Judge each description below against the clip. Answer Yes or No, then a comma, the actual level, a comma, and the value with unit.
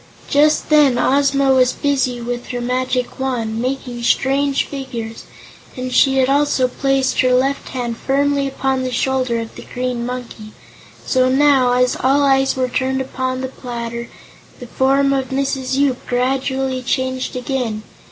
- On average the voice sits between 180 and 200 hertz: No, very high, 260 Hz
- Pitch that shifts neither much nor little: No, narrow, 1.5 semitones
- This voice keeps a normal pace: Yes, average, 150 wpm